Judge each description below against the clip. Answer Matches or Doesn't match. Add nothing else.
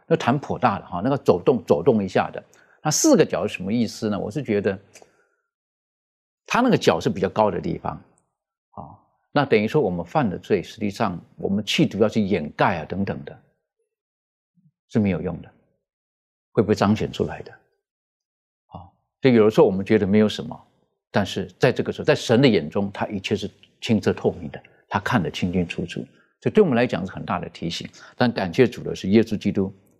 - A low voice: Matches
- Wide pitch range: Doesn't match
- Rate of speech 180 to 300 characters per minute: Matches